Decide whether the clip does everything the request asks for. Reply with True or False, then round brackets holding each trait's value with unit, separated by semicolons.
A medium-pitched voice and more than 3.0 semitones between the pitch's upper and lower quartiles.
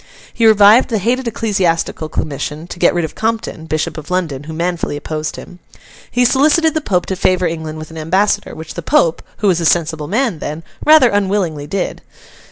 True (180 Hz; 5.4 semitones)